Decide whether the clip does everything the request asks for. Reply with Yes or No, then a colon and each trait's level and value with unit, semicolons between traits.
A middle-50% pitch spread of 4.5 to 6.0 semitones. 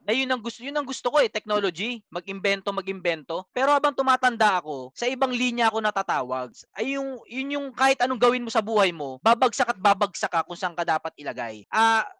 Yes: average, 4.9 semitones